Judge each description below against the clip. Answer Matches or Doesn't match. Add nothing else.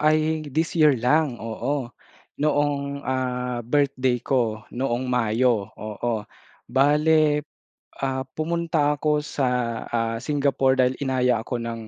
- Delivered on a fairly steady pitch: Doesn't match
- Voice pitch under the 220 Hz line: Matches